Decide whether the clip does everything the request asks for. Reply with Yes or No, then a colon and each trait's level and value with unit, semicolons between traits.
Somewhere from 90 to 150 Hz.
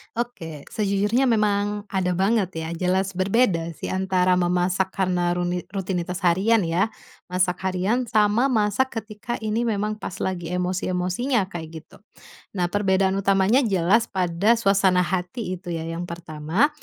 No: high, 190 Hz